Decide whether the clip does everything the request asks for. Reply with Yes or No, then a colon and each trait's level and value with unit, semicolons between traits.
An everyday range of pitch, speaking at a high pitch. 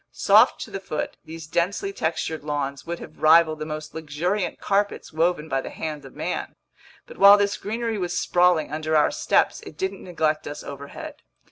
No: average, 3.7 semitones; medium, 160 Hz